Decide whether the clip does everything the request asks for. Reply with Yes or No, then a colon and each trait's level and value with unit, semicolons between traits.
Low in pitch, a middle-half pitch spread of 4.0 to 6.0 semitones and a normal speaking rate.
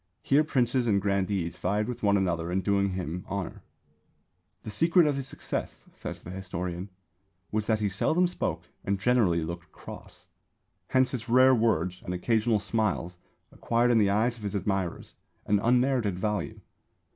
Yes: low, 105 Hz; average, 4.4 semitones; average, 160 wpm